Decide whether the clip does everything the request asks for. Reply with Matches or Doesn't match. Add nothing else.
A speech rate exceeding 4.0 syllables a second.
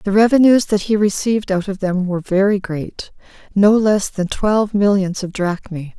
Matches